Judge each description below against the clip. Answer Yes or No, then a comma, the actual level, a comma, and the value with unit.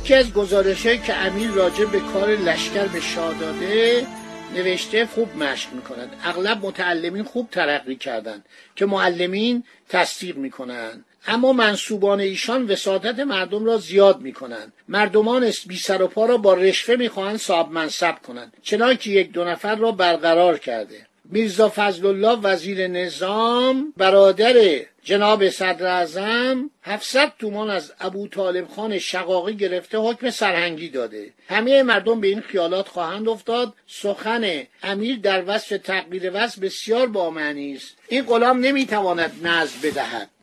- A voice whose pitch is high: Yes, high, 200 Hz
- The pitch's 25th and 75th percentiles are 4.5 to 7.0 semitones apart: No, average, 3.9 semitones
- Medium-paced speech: Yes, average, 140 wpm